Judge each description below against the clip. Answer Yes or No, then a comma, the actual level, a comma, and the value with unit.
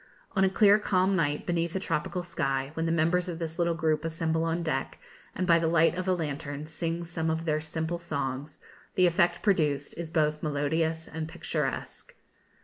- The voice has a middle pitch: Yes, medium, 165 Hz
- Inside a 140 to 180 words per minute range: No, average, 190 wpm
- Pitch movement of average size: No, narrow, 2.0 semitones